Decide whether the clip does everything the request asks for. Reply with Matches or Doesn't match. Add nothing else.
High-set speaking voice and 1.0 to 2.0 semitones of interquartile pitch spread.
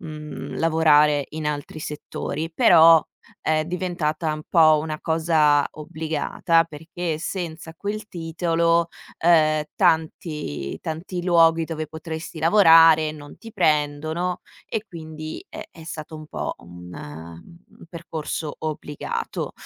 Doesn't match